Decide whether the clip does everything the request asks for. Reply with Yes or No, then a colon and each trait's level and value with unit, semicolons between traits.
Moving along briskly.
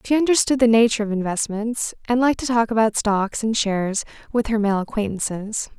No: average, 185 wpm